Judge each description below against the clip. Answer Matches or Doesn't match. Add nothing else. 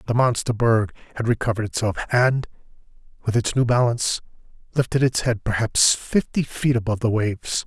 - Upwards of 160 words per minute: Doesn't match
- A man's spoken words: Matches